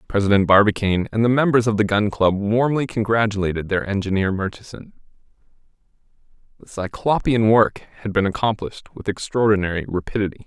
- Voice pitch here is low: Yes, low, 105 Hz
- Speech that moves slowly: Yes, slow, 130 wpm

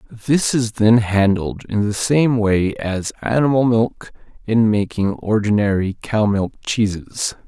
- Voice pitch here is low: Yes, low, 110 Hz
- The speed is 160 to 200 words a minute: No, slow, 135 wpm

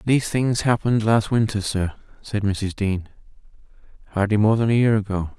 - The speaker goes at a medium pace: Yes, average, 165 wpm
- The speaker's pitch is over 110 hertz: No, low, 105 Hz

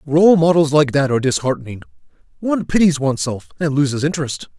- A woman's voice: No, male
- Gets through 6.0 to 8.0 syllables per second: Yes, 6.5 syllables/s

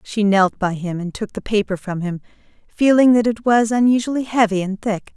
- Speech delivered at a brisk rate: Yes, fast, 210 wpm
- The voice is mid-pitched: No, high, 210 Hz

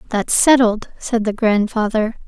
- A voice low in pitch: No, high, 220 Hz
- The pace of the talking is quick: No, slow, 130 wpm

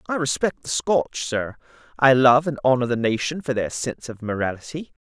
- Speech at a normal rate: Yes, average, 190 wpm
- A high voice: No, low, 135 Hz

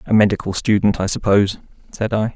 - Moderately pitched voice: No, low, 105 Hz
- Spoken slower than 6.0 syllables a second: No, 6.2 syllables/s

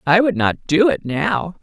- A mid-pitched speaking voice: Yes, medium, 175 Hz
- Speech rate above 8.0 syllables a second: No, 4.1 syllables/s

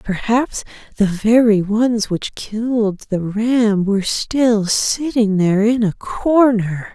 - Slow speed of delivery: Yes, slow, 130 wpm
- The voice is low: No, high, 215 Hz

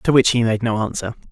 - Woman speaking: No, male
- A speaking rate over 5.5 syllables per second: Yes, 6.1 syllables/s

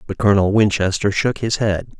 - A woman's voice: No, male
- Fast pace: No, average, 180 wpm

